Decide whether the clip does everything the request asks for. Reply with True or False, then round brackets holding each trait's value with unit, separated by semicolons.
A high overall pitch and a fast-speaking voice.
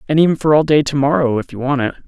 False (140 Hz; 320 wpm)